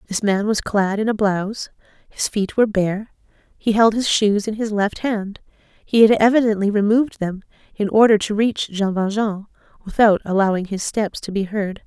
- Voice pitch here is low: No, high, 210 Hz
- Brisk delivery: No, average, 185 wpm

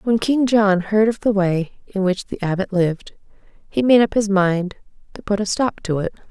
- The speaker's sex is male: No, female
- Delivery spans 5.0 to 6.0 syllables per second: No, 4.7 syllables/s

